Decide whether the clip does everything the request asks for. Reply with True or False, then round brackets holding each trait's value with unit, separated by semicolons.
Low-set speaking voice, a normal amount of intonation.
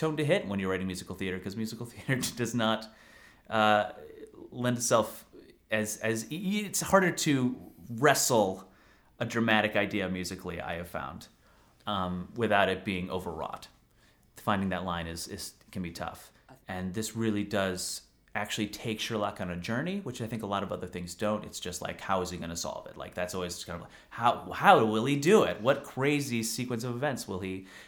True (105 Hz; 4.5 semitones)